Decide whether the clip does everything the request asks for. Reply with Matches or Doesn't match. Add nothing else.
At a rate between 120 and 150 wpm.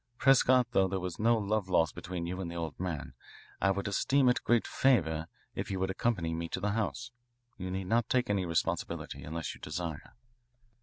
Doesn't match